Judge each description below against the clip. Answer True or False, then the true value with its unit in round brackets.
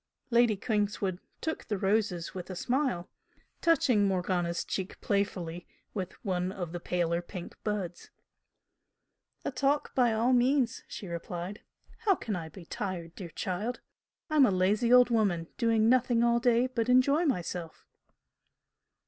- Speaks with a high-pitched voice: True (205 Hz)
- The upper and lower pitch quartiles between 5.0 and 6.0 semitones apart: True (5.3 semitones)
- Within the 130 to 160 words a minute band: True (140 wpm)